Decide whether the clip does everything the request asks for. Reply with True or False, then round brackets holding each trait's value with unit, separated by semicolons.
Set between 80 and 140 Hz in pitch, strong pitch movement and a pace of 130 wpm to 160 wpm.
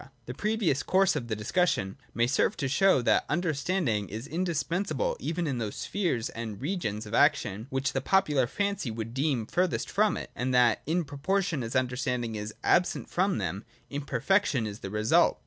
False (135 Hz; 7.7 semitones; 175 wpm)